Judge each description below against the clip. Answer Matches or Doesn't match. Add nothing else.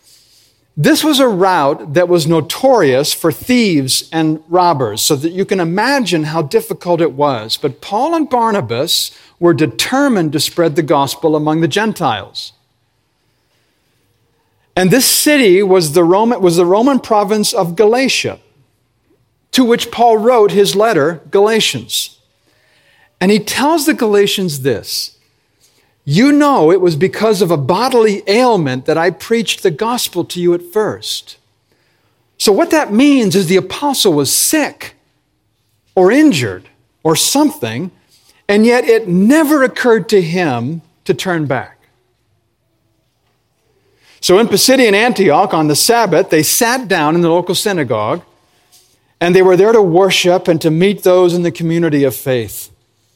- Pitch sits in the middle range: Matches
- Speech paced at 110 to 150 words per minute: Matches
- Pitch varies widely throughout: Matches